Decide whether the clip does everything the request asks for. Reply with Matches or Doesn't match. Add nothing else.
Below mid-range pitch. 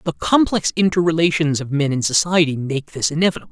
Doesn't match